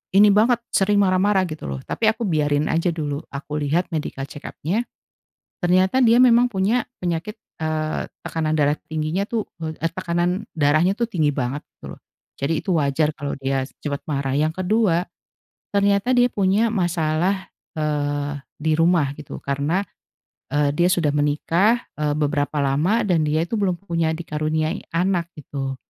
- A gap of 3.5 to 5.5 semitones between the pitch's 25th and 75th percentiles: Yes, average, 4.5 semitones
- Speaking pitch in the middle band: Yes, medium, 160 Hz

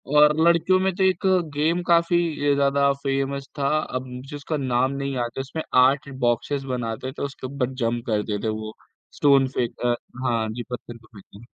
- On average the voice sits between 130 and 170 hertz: Yes, low, 135 Hz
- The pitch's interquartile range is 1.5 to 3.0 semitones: No, average, 3.5 semitones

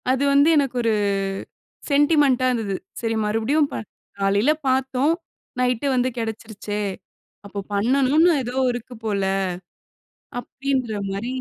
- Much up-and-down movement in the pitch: No, average, 3.8 semitones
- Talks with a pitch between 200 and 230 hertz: No, very high, 250 Hz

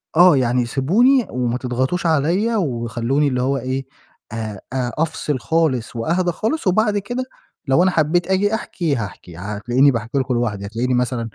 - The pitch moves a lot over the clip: Yes, wide, 6.6 semitones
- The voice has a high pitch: No, low, 135 Hz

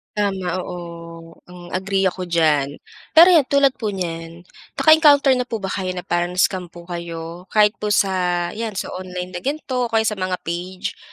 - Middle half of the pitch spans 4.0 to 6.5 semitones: No, average, 3.6 semitones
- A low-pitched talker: No, medium, 185 Hz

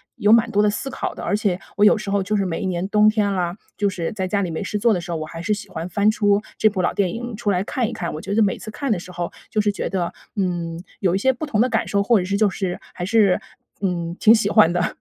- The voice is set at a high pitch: Yes, high, 200 Hz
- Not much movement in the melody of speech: No, average, 3.0 semitones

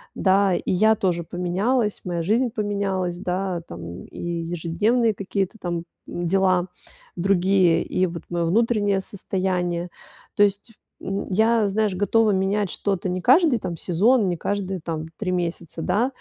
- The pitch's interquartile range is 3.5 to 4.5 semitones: No, average, 2.9 semitones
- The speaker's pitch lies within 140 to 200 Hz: Yes, high, 190 Hz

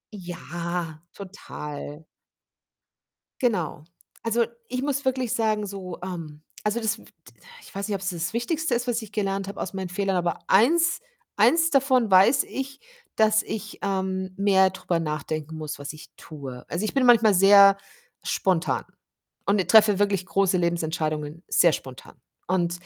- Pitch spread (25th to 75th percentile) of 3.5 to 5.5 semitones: Yes, average, 4.3 semitones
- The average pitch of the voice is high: Yes, high, 195 Hz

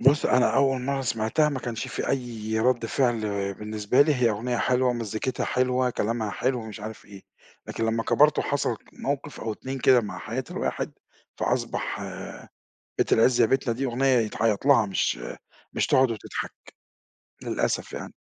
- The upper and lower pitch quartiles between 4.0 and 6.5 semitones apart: No, average, 3.0 semitones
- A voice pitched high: No, low, 120 Hz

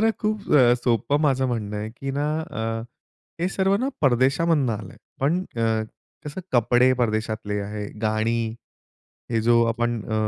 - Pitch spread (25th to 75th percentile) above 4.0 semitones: Yes, average, 4.5 semitones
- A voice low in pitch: Yes, low, 120 Hz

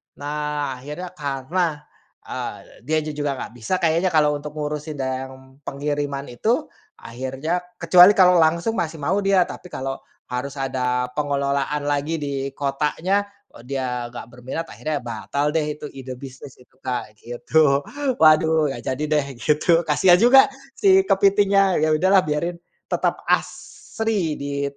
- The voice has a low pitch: No, medium, 150 Hz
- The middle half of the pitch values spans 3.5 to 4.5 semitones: Yes, average, 3.9 semitones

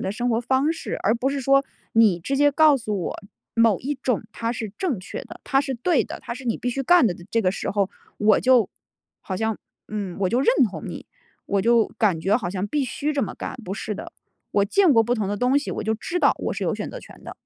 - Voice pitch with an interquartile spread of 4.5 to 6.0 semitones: Yes, average, 4.8 semitones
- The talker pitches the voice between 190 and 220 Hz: No, high, 230 Hz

